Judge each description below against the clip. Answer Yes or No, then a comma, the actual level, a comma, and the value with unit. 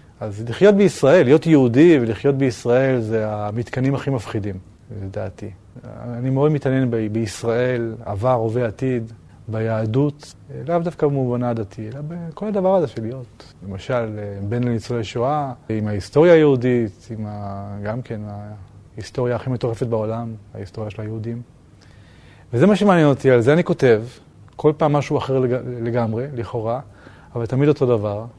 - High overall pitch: No, low, 120 Hz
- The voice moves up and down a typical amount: Yes, average, 3.7 semitones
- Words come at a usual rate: Yes, average, 140 wpm